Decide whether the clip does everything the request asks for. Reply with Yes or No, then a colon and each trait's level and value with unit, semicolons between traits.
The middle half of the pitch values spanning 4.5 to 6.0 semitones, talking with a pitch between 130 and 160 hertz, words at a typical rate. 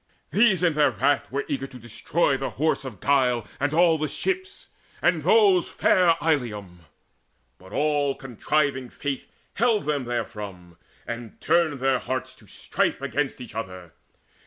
Yes: average, 4.9 semitones; low, 135 Hz; average, 150 wpm